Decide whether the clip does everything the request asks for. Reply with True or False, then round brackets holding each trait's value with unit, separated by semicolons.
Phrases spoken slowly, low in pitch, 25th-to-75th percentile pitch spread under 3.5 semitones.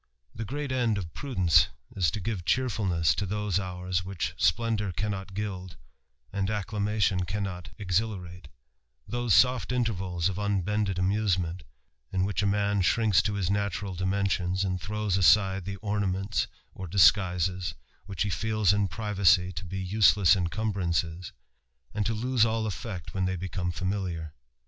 False (145 wpm; 95 Hz; 2.5 semitones)